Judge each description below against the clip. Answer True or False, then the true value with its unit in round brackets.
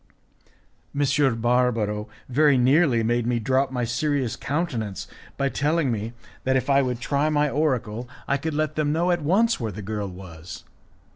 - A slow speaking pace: False (165 wpm)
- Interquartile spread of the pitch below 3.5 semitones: False (4.4 semitones)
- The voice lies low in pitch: True (130 Hz)